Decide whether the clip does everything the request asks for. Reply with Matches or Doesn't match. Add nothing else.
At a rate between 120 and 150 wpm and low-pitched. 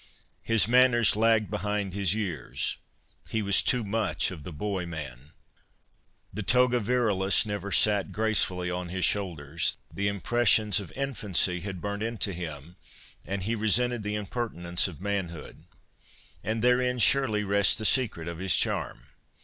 Matches